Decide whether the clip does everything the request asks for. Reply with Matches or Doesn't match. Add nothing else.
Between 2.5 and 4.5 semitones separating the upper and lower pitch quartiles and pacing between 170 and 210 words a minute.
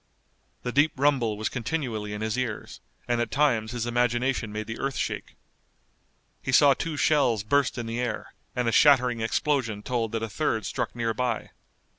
Matches